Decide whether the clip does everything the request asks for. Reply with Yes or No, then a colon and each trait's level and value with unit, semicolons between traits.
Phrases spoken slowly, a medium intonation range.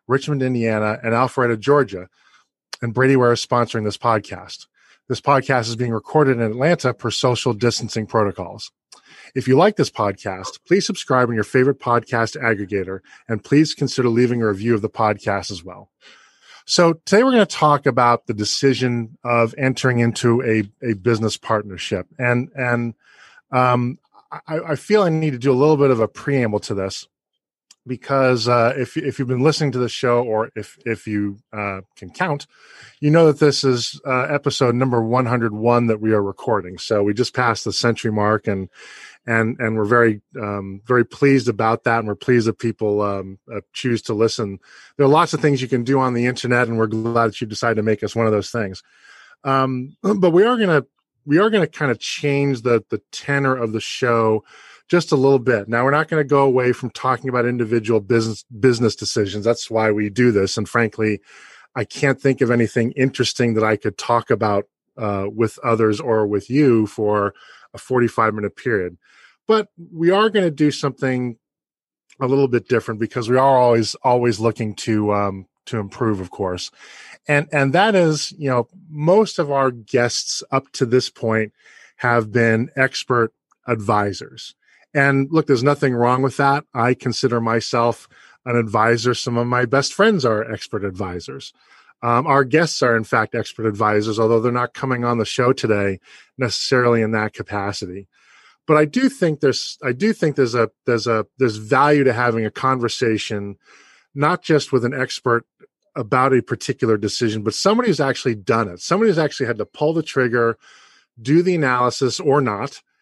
No: average, 185 wpm; average, 3.5 semitones